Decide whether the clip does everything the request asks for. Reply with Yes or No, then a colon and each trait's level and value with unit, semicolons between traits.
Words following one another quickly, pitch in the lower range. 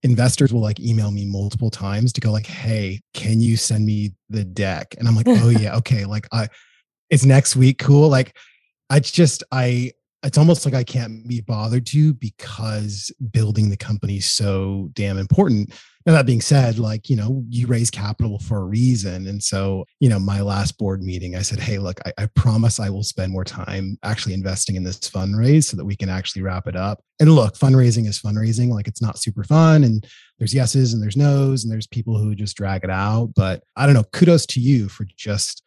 Yes: fast, 215 wpm; low, 110 Hz